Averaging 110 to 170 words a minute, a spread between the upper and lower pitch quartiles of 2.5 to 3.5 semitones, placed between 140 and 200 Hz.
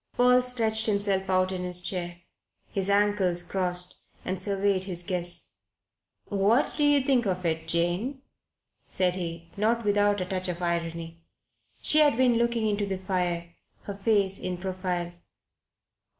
Yes: average, 150 wpm; average, 2.9 semitones; high, 190 Hz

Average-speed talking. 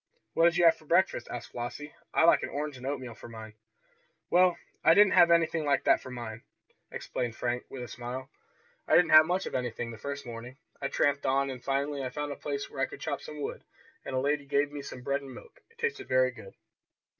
No: fast, 235 wpm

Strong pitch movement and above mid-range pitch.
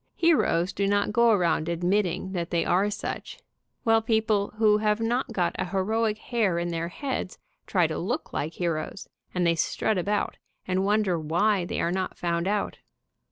No: average, 3.9 semitones; high, 195 Hz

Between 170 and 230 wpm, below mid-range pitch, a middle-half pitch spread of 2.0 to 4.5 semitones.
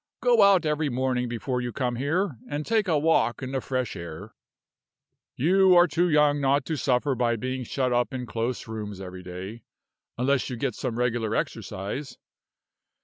Yes: average, 175 wpm; low, 130 Hz; average, 4.1 semitones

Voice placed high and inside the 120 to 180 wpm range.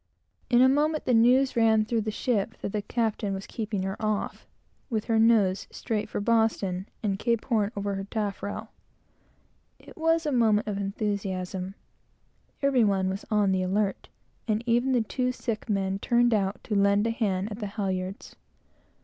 Yes: high, 215 Hz; average, 175 wpm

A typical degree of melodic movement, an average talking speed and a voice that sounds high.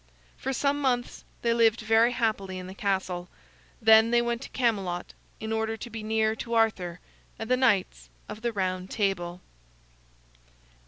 Yes: average, 3.5 semitones; average, 160 wpm; high, 220 Hz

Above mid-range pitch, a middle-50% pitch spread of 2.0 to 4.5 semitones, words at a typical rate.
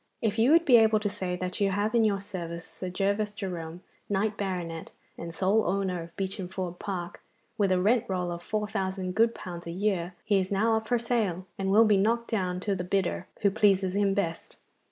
No: high, 195 Hz; average, 2.7 semitones; fast, 215 wpm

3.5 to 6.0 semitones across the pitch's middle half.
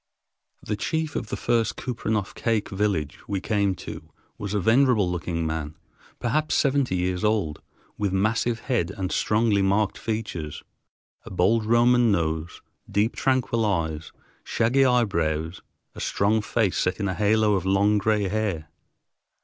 Yes: average, 3.8 semitones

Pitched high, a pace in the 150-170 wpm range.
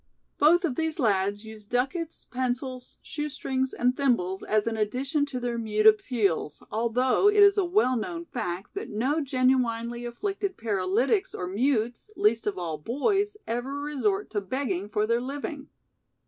Yes: very high, 250 Hz; average, 155 wpm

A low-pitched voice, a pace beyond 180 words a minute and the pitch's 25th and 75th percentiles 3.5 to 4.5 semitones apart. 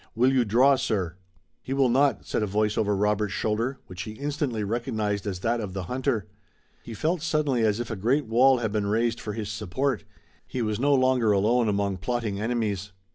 Yes: low, 110 Hz; average, 200 wpm; average, 3.8 semitones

